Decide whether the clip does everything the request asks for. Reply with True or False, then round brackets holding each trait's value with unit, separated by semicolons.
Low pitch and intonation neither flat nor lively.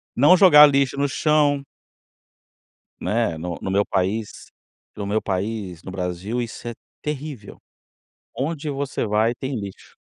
False (115 Hz; 6.2 semitones)